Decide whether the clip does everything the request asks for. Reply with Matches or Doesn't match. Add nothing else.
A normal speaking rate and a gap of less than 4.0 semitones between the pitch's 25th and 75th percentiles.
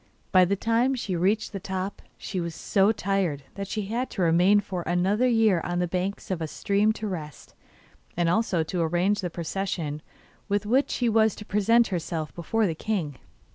Matches